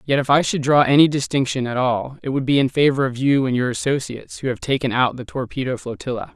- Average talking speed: No, fast, 245 wpm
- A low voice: Yes, low, 130 Hz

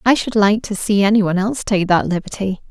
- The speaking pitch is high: Yes, high, 205 Hz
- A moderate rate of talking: No, fast, 220 wpm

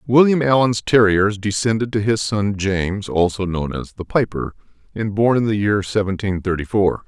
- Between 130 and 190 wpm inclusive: Yes, average, 180 wpm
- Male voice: Yes, male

